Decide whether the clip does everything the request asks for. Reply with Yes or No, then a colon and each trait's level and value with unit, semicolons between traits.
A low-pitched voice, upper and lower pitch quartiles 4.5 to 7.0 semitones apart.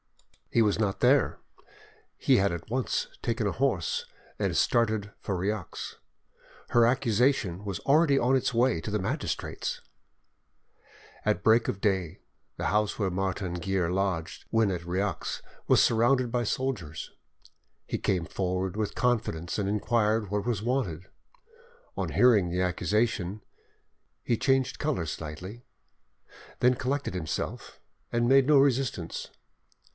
Yes: low, 105 Hz; average, 4.9 semitones